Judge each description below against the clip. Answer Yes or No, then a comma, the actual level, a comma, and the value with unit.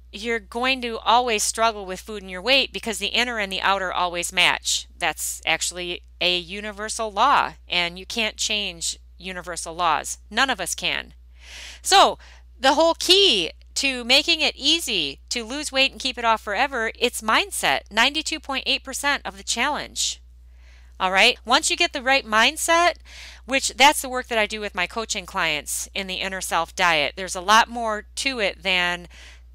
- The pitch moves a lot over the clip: Yes, wide, 6.4 semitones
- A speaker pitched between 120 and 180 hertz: No, high, 210 Hz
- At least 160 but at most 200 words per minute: Yes, average, 175 wpm